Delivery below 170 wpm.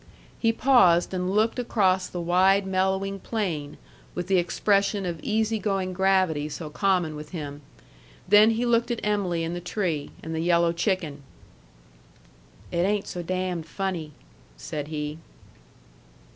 Yes: average, 145 wpm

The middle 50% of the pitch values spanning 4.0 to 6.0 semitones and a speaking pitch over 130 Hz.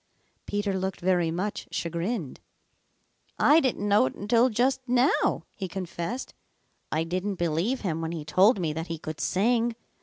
Yes: wide, 5.4 semitones; high, 190 Hz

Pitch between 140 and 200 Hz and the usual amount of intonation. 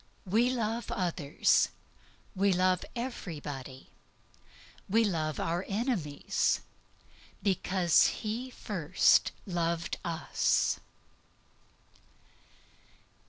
Yes: medium, 185 Hz; average, 4.7 semitones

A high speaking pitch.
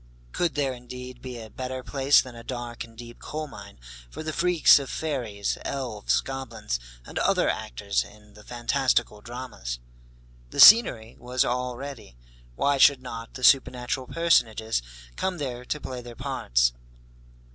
No: low, 125 Hz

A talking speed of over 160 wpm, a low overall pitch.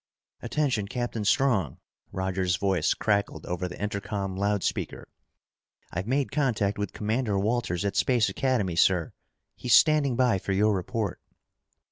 No: slow, 135 wpm; low, 105 Hz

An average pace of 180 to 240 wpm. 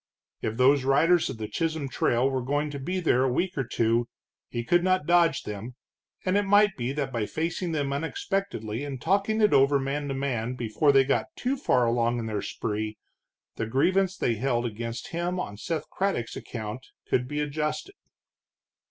Yes: average, 185 wpm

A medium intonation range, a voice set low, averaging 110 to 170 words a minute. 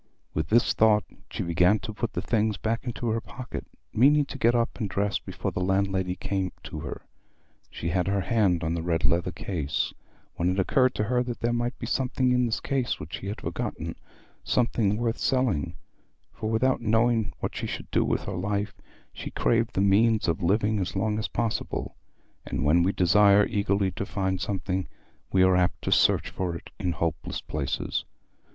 No: average, 4.1 semitones; low, 100 Hz; average, 190 wpm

